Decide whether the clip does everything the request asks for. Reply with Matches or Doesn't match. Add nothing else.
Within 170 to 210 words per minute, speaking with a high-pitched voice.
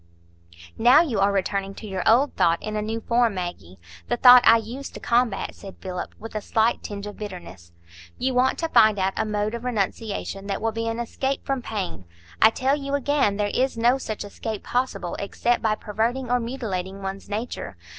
Matches